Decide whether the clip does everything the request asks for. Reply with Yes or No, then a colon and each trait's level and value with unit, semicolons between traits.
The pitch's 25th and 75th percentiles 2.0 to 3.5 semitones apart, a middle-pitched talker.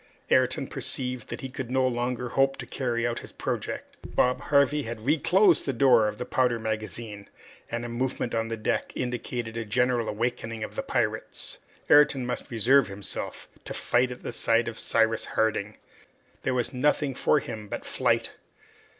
No: narrow, 2.4 semitones; low, 120 Hz